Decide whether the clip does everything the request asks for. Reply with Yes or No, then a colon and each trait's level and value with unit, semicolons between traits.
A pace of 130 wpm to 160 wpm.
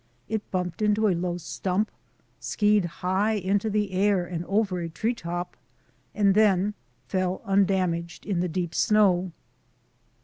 Yes: average, 140 wpm